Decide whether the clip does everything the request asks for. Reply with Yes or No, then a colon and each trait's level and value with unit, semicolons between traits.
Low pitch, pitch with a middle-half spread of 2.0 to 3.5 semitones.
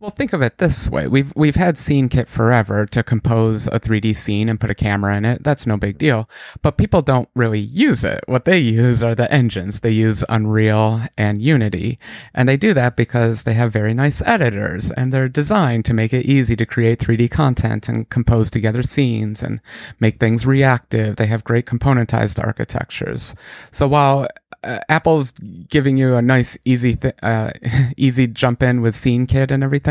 Yes: low, 120 Hz; average, 3.0 semitones